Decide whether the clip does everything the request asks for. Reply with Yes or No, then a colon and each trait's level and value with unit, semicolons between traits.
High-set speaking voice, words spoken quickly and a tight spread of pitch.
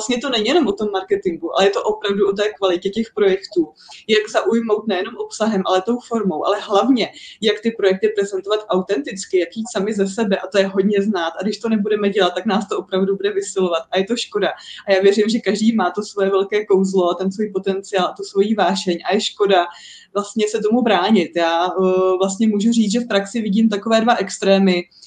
Yes: high, 200 Hz; fast, 215 wpm; narrow, 2.1 semitones